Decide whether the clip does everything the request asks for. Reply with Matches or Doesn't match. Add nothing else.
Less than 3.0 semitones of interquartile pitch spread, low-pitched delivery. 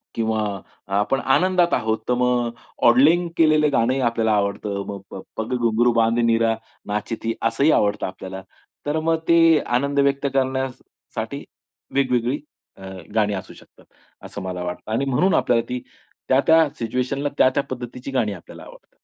Doesn't match